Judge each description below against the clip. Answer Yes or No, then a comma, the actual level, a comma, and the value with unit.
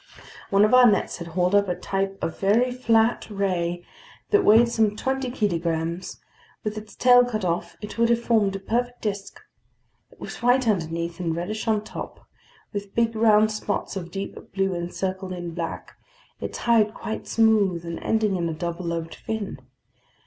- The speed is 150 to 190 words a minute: Yes, average, 175 wpm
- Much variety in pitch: No, average, 4.1 semitones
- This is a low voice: No, high, 200 Hz